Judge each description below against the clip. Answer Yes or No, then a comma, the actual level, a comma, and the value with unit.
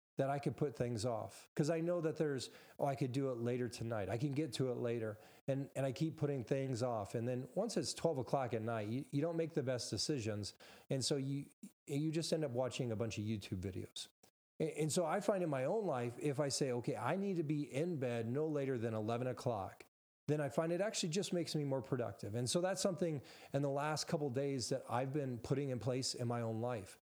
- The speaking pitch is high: No, medium, 140 Hz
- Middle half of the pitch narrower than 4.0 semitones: No, average, 4.4 semitones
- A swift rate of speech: Yes, fast, 250 wpm